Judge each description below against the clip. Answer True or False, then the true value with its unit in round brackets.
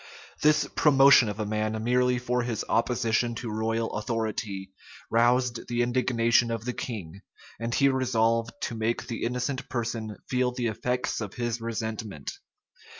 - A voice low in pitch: True (115 Hz)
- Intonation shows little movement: True (2.0 semitones)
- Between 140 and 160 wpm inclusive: True (150 wpm)